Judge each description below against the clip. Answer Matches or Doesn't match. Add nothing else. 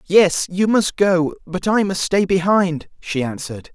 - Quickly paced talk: Doesn't match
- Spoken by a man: Matches